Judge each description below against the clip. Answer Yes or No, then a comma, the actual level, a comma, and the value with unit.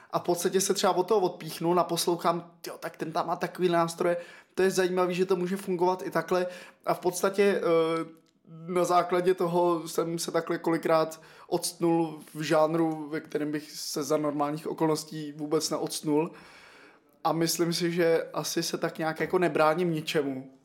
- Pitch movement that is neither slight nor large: No, narrow, 1.9 semitones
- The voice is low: No, medium, 170 Hz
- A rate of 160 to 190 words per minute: Yes, fast, 170 wpm